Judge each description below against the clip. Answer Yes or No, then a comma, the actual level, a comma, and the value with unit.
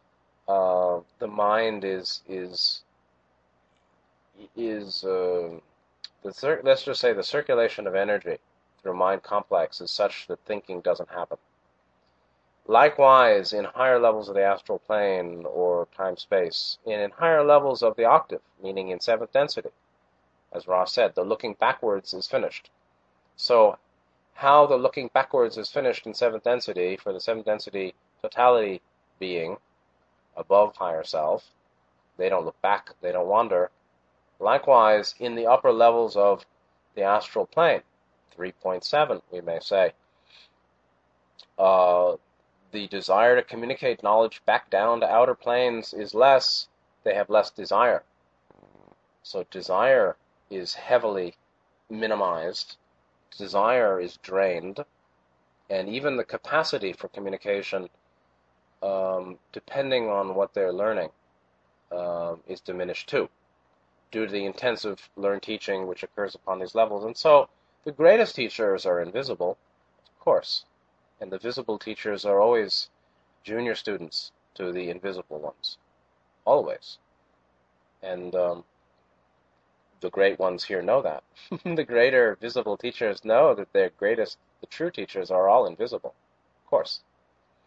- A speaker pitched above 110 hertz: No, very low, 90 Hz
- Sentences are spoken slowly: Yes, slow, 130 wpm